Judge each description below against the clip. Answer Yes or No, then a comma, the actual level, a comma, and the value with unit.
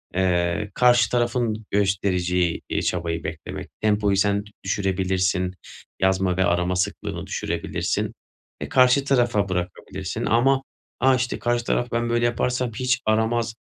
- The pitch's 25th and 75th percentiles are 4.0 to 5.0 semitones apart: Yes, average, 4.5 semitones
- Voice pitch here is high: No, low, 105 Hz